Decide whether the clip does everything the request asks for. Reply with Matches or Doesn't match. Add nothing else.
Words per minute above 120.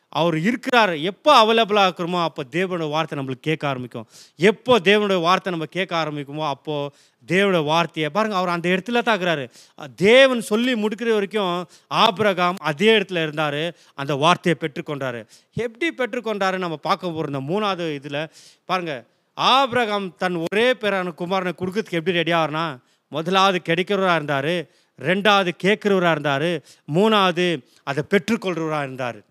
Matches